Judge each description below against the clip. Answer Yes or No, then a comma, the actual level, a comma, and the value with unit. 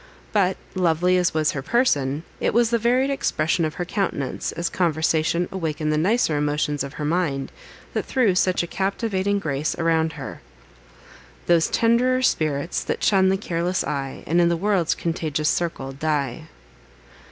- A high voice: No, medium, 170 Hz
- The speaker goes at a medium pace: Yes, average, 160 wpm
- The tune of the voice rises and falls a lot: No, average, 4.0 semitones